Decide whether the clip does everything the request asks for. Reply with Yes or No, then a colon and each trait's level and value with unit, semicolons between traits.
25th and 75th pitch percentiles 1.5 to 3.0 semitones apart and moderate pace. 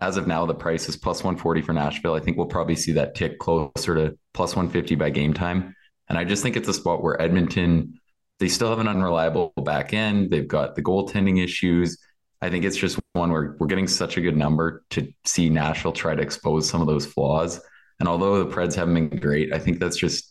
No: narrow, 2.5 semitones; fast, 230 wpm